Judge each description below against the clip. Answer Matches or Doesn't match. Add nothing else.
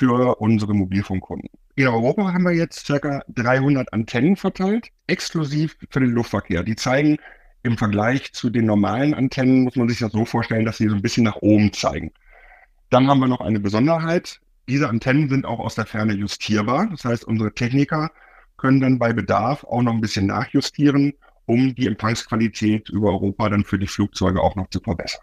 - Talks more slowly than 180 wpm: Doesn't match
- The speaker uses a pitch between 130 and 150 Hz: Doesn't match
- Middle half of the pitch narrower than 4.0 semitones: Doesn't match